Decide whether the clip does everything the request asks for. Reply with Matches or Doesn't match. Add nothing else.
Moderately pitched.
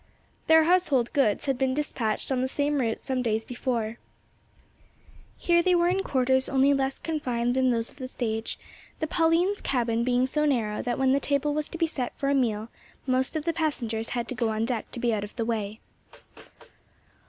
Doesn't match